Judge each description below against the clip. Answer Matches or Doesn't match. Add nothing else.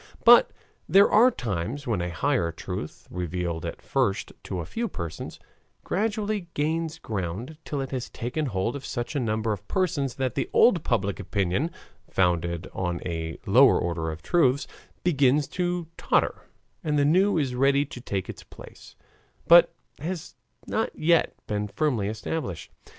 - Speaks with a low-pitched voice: Matches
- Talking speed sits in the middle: Matches